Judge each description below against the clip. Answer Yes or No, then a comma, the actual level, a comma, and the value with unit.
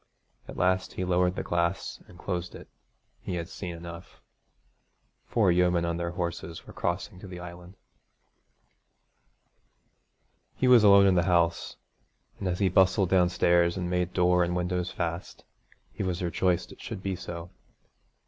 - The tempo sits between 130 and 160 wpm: Yes, average, 155 wpm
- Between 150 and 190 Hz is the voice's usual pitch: No, very low, 90 Hz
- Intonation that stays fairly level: Yes, narrow, 1.3 semitones